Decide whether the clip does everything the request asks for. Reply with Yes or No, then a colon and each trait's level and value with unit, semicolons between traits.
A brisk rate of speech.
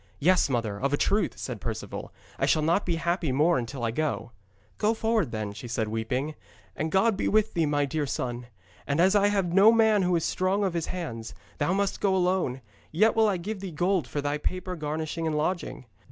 Yes: fast, 215 wpm